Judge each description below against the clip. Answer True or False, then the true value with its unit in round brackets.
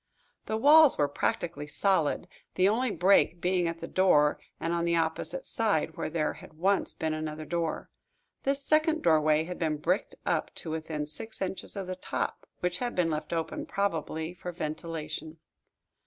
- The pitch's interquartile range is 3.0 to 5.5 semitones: True (3.9 semitones)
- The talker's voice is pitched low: False (170 Hz)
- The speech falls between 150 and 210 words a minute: True (170 wpm)